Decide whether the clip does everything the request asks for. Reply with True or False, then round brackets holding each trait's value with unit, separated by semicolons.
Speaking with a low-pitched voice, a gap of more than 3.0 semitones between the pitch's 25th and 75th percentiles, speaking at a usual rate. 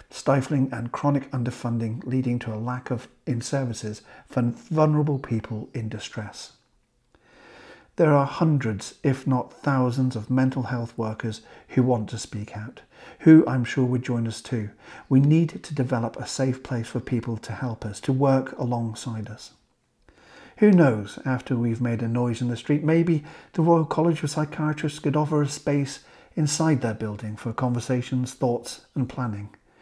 True (125 Hz; 3.6 semitones; 165 wpm)